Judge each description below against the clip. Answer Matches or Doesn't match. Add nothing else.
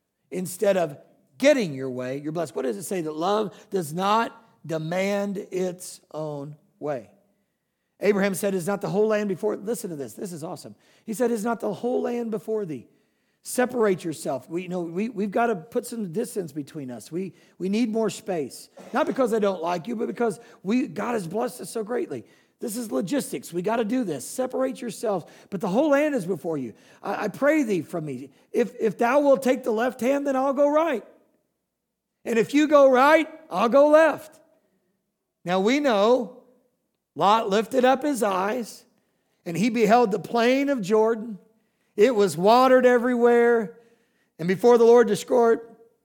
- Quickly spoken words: Doesn't match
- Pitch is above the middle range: Matches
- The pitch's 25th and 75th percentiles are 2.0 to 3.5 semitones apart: Doesn't match